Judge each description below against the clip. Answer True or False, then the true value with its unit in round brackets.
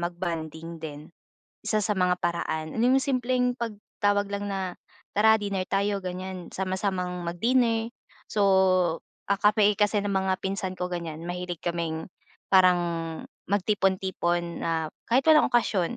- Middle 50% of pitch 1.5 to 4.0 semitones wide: True (3.1 semitones)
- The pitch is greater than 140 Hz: True (190 Hz)